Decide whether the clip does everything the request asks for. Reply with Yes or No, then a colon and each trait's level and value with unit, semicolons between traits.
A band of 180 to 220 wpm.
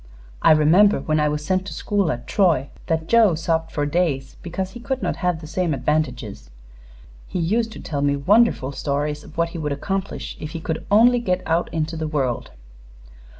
Yes: average, 195 wpm